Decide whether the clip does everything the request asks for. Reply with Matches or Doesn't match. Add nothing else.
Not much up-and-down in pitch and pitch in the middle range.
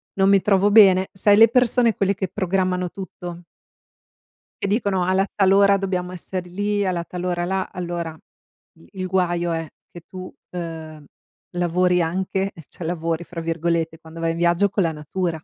Matches